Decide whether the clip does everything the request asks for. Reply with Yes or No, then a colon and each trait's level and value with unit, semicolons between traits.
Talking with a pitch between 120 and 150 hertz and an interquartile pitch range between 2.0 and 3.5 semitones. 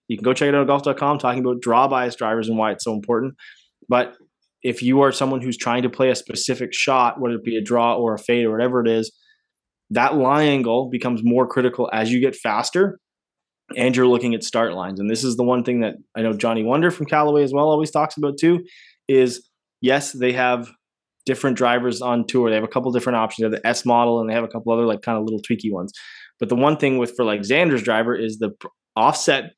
Yes: low, 125 Hz; narrow, 2.6 semitones